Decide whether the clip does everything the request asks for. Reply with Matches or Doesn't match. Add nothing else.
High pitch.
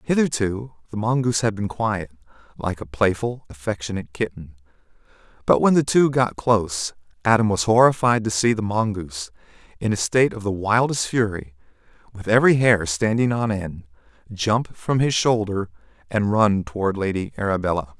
Doesn't match